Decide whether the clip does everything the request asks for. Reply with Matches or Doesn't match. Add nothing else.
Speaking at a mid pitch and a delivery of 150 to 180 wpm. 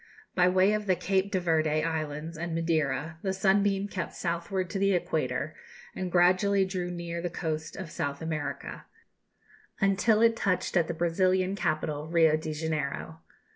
Matches